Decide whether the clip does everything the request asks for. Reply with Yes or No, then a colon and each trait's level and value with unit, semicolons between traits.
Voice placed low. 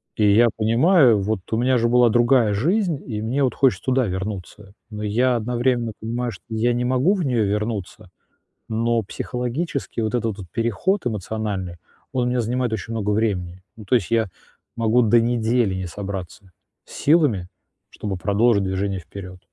Yes: low, 115 Hz